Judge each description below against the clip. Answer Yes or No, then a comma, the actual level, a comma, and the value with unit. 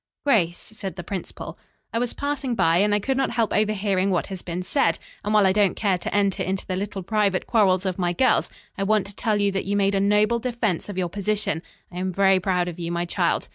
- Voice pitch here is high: Yes, high, 195 Hz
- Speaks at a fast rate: Yes, fast, 245 wpm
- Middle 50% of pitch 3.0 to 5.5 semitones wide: No, narrow, 2.5 semitones